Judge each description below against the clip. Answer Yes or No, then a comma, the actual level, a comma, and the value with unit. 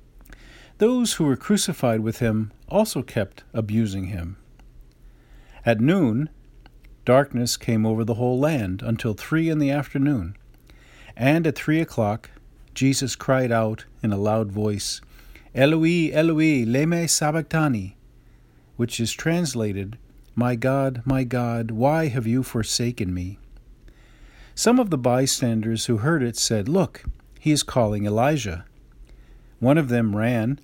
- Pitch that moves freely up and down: No, average, 4.7 semitones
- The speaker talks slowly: Yes, slow, 130 wpm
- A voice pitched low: Yes, low, 125 Hz